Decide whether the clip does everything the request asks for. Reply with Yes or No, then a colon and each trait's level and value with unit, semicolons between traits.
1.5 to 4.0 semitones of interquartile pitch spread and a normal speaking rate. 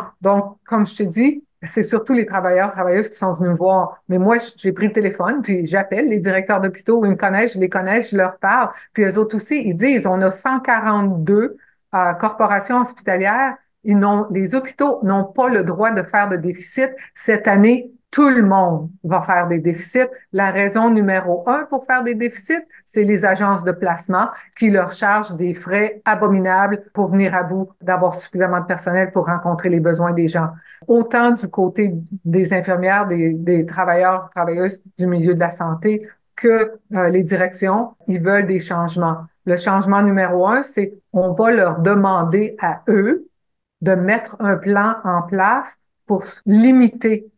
Yes: average, 3.3 semitones; average, 180 wpm